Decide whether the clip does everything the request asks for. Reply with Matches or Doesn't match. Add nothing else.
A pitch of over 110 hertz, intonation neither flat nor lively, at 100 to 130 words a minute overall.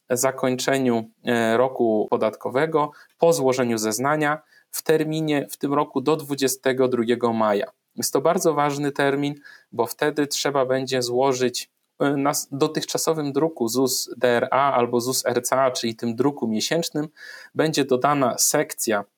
Matches